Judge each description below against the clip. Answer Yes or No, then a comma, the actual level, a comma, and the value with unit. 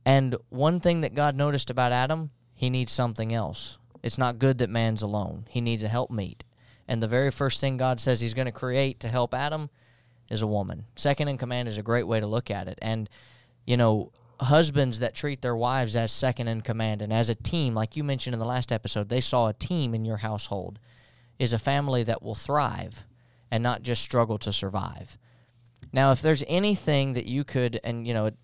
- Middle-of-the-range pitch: No, low, 120 Hz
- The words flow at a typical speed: No, fast, 215 wpm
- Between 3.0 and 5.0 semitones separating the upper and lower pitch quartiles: No, narrow, 2.5 semitones